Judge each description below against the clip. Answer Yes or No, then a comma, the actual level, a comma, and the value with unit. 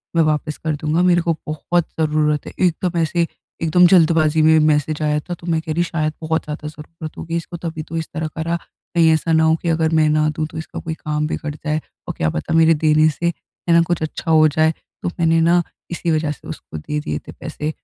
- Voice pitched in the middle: Yes, medium, 160 Hz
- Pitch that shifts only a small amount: Yes, narrow, 1.4 semitones